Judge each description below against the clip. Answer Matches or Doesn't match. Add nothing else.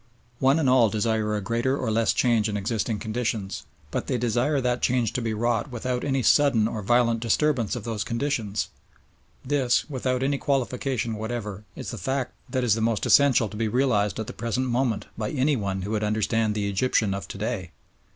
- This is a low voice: Matches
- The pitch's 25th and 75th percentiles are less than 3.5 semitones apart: Matches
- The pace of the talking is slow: Doesn't match